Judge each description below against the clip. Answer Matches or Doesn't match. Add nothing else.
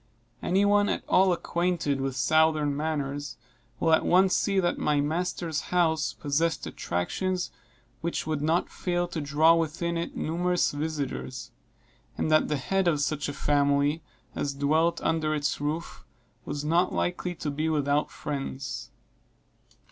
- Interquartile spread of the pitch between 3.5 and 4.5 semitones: Doesn't match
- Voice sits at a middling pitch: Matches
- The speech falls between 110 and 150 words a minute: Matches